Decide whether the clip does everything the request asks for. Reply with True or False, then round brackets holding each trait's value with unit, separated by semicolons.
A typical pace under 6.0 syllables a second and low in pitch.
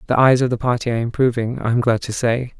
False (6.7 syllables/s; 120 Hz)